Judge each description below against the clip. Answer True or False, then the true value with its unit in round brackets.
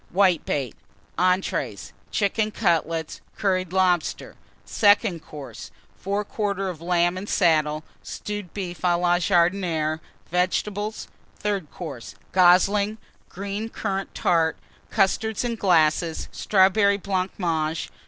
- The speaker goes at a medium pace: False (105 wpm)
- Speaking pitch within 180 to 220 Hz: True (185 Hz)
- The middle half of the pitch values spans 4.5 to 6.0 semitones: False (3.1 semitones)